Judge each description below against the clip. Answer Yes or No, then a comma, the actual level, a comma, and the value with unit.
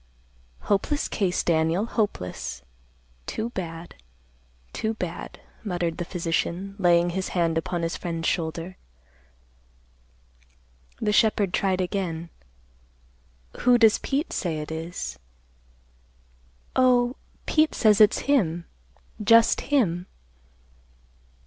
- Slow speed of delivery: Yes, slow, 100 wpm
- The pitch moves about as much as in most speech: Yes, average, 4.6 semitones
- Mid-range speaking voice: Yes, medium, 180 Hz